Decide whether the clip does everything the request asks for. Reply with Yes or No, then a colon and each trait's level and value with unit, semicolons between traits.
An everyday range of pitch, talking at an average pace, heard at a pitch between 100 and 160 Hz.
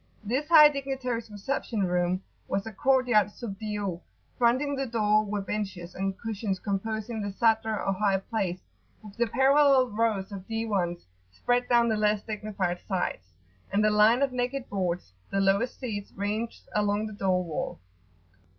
No: average, 3.3 semitones; average, 160 wpm; high, 210 Hz